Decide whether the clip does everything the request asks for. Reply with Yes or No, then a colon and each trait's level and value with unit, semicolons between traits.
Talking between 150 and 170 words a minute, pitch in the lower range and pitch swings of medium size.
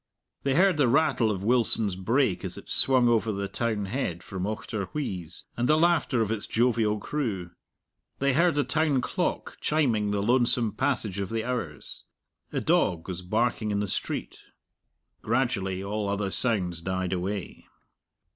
Yes: average, 155 wpm; low, 110 Hz; average, 4.6 semitones